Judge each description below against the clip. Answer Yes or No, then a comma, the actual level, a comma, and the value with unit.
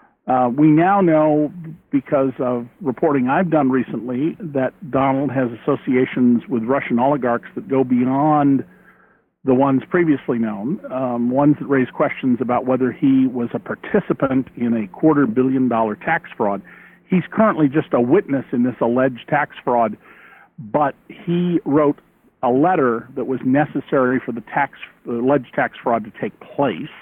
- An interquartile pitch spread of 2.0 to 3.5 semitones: Yes, average, 3.2 semitones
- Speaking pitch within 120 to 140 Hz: Yes, low, 135 Hz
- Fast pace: No, average, 155 wpm